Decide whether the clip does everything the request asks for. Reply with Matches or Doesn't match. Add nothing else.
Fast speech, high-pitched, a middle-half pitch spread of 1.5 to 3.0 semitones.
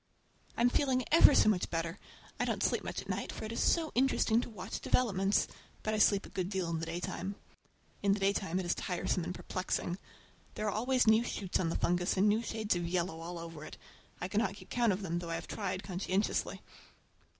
Doesn't match